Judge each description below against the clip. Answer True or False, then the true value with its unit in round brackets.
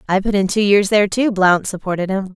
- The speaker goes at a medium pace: False (255 wpm)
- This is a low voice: False (195 Hz)